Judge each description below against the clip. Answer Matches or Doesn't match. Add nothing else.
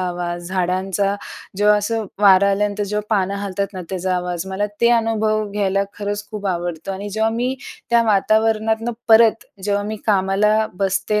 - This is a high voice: Matches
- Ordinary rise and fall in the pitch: Doesn't match